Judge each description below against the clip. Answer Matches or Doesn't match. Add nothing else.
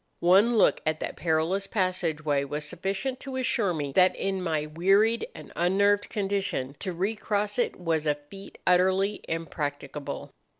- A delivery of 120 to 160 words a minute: Matches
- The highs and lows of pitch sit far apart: Doesn't match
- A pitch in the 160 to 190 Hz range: Matches